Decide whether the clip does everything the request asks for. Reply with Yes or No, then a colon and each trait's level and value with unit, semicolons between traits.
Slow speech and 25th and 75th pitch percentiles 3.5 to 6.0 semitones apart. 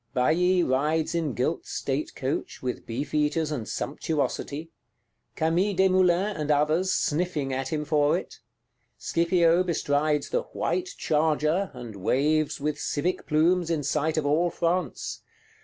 No: slow, 130 wpm; average, 3.0 semitones